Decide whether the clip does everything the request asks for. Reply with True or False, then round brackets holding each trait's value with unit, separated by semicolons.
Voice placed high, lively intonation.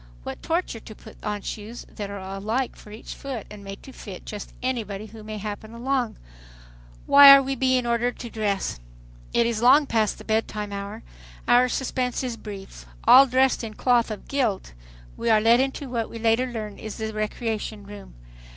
False (225 Hz; 3.2 semitones)